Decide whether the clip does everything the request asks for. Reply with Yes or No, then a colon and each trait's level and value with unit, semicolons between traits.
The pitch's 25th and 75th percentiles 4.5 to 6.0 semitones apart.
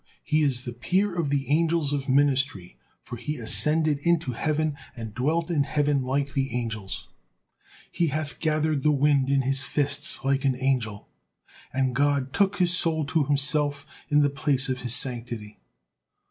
No: average, 2.8 semitones